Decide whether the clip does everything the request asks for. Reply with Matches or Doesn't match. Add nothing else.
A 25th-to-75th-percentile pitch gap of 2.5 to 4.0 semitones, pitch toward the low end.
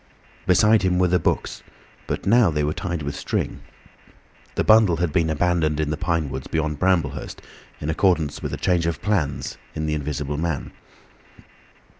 Matches